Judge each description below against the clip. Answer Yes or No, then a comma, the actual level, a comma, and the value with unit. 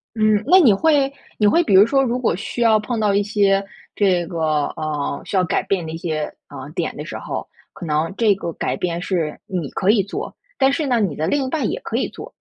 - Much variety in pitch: Yes, wide, 5.7 semitones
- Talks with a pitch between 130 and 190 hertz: No, high, 200 Hz